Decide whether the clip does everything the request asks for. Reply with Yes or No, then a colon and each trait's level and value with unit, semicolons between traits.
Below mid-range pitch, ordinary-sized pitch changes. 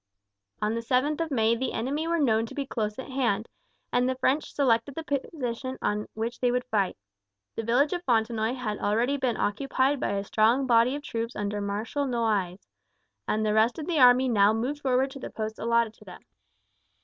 No: high, 235 Hz; average, 3.5 semitones